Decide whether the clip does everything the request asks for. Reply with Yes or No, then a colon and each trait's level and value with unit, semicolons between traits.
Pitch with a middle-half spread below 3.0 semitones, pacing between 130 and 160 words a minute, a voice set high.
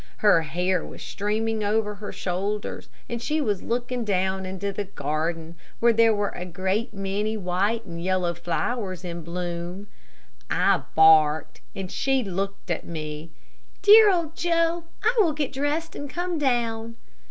No: average, 5.1 semitones; average, 155 wpm; high, 200 Hz